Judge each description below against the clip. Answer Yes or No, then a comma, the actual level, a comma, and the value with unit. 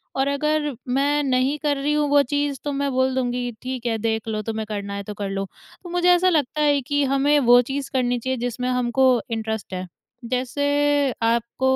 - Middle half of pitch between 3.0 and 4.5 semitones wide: Yes, average, 3.6 semitones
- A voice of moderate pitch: No, very high, 260 Hz